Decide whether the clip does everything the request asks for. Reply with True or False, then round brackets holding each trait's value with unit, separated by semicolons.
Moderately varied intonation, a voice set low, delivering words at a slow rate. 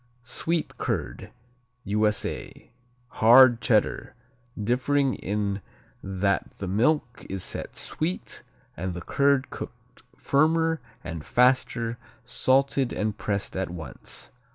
True (4.9 semitones; 120 Hz; 105 wpm)